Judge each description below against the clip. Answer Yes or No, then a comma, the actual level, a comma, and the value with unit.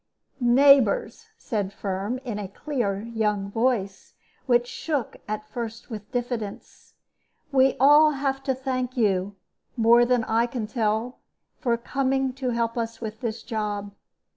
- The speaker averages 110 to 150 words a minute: Yes, average, 140 wpm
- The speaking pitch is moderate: No, high, 235 Hz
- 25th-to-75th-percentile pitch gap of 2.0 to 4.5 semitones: Yes, average, 3.4 semitones